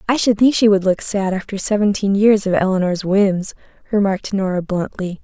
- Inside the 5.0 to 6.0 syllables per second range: Yes, 5.3 syllables/s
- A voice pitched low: No, high, 200 Hz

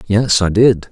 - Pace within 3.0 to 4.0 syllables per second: Yes, 3.9 syllables/s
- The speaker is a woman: No, male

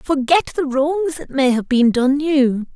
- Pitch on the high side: Yes, very high, 280 Hz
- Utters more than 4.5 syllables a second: No, 4.0 syllables/s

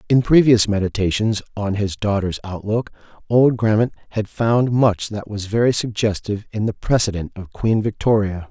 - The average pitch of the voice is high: No, low, 105 Hz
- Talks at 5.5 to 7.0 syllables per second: No, 4.9 syllables/s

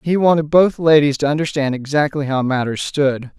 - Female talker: No, male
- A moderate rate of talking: Yes, average, 175 wpm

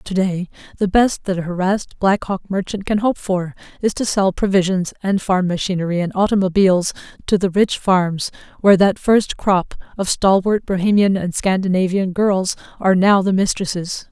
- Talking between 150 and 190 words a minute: Yes, average, 170 wpm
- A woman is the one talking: Yes, female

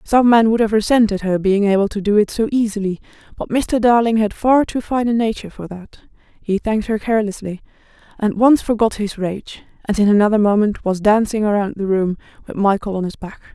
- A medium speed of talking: No, fast, 210 wpm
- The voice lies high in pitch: Yes, high, 210 Hz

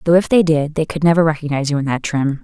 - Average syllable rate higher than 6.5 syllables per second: Yes, 6.9 syllables/s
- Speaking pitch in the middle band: Yes, medium, 155 Hz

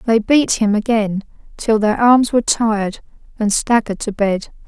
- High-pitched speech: Yes, high, 220 Hz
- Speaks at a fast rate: No, average, 165 wpm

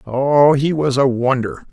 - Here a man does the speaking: Yes, male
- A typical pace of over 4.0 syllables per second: No, 3.9 syllables/s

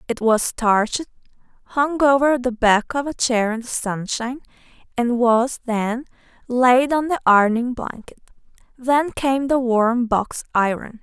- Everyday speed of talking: Yes, average, 145 wpm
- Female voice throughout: Yes, female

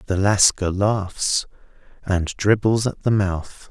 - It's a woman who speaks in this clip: No, male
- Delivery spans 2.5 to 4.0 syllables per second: Yes, 3.3 syllables/s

